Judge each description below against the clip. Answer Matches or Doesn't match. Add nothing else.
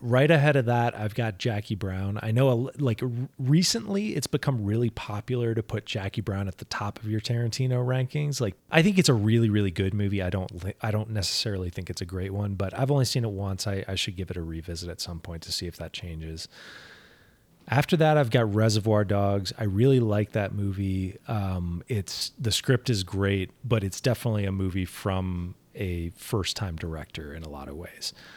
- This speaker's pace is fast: Matches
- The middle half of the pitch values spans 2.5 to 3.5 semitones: Doesn't match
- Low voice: Matches